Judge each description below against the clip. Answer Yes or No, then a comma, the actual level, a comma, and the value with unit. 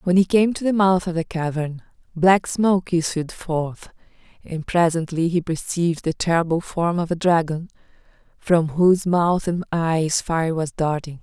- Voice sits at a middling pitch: Yes, medium, 170 Hz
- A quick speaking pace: No, average, 165 wpm